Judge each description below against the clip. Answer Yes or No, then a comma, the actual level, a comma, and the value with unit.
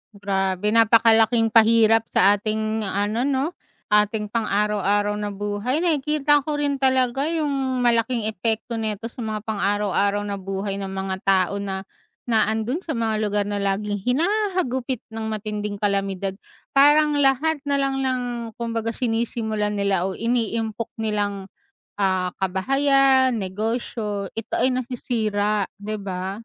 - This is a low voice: No, high, 220 Hz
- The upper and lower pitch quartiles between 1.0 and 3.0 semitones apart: No, average, 3.7 semitones